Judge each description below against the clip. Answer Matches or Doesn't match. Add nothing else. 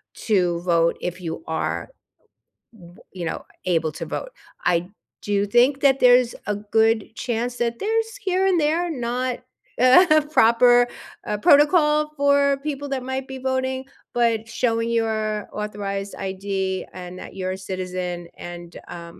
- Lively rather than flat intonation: Matches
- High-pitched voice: Matches